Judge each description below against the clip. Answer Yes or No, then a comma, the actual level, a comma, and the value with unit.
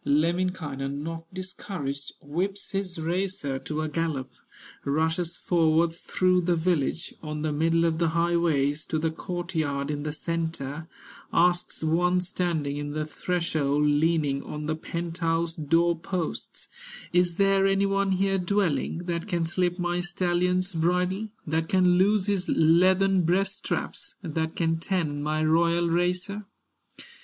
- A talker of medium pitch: Yes, medium, 170 Hz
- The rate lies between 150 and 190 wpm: No, average, 140 wpm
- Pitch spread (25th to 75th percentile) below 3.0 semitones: Yes, narrow, 2.5 semitones